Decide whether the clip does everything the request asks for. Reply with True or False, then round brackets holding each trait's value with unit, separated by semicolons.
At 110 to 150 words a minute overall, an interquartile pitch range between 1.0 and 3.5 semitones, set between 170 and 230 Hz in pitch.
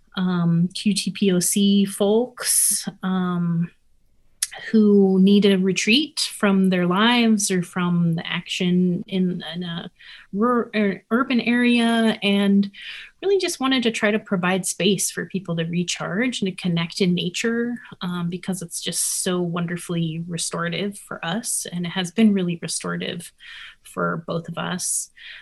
True (135 wpm; 3.1 semitones; 190 Hz)